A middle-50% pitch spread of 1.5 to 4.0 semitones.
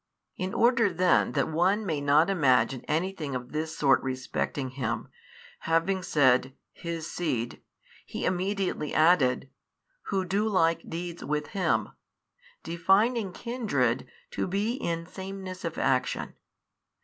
No: wide, 5.4 semitones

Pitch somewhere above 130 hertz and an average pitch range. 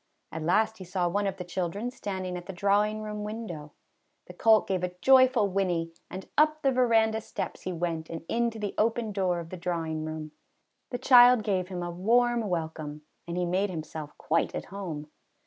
Yes: high, 190 Hz; average, 4.4 semitones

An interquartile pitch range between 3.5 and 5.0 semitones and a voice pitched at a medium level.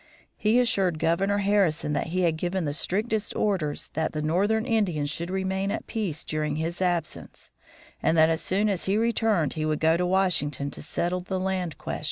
Yes: average, 3.9 semitones; medium, 180 Hz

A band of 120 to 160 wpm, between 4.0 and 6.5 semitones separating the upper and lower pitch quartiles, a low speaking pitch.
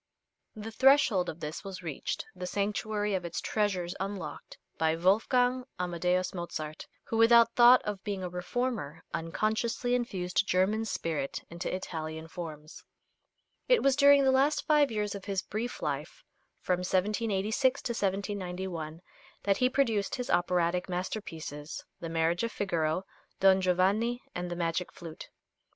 No: average, 140 wpm; average, 4.6 semitones; high, 190 Hz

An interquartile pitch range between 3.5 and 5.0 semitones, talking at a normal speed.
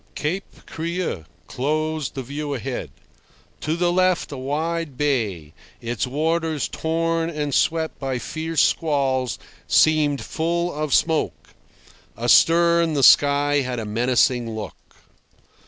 No: average, 4.0 semitones; slow, 120 wpm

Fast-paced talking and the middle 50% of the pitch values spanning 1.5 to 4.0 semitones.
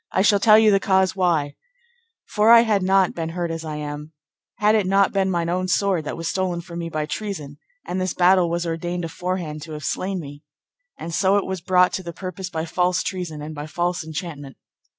Yes: fast, 220 wpm; average, 2.8 semitones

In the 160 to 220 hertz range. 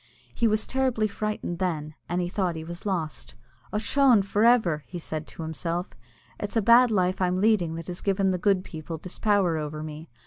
Yes: medium, 185 Hz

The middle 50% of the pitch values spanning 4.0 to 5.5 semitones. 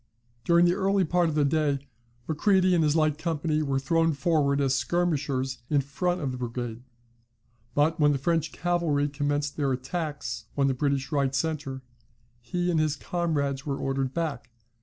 No: average, 3.3 semitones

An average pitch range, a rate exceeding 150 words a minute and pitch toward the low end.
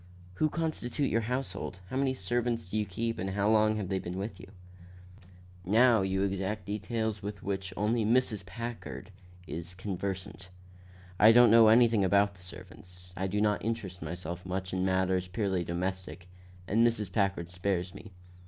Yes: average, 3.3 semitones; average, 165 wpm; low, 100 Hz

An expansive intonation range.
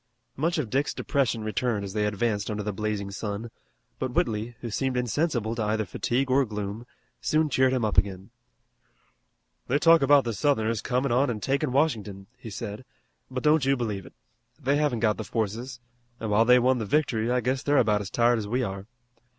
No: average, 3.9 semitones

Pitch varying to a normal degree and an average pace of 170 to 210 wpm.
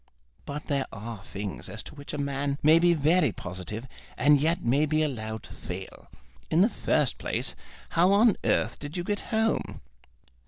No: wide, 6.3 semitones; average, 180 wpm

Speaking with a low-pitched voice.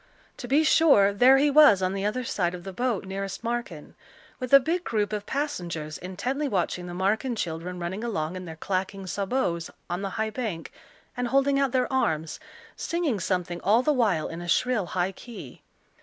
No: high, 200 Hz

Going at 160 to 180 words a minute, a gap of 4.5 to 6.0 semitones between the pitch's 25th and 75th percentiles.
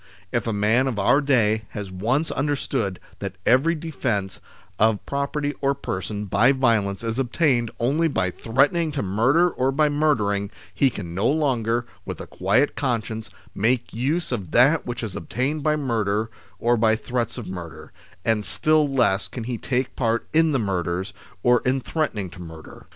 Yes: average, 175 wpm; average, 5.1 semitones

